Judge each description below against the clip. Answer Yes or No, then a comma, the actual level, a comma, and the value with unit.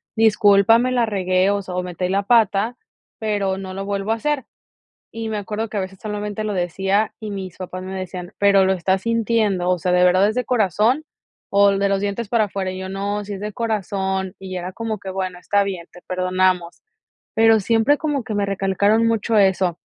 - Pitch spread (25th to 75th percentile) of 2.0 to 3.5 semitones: Yes, narrow, 2.6 semitones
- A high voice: Yes, high, 200 Hz